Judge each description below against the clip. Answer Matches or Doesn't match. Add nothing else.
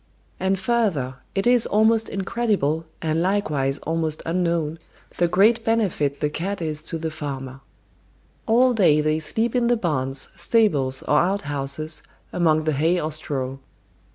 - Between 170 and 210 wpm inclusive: Doesn't match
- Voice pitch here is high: Doesn't match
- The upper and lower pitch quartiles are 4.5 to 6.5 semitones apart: Matches